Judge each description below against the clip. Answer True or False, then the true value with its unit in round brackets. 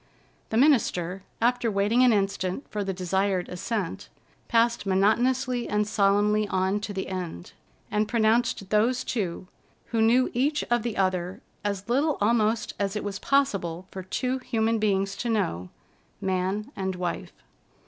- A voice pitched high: True (210 Hz)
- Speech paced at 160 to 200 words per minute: False (150 wpm)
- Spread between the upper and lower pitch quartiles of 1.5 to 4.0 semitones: True (3.6 semitones)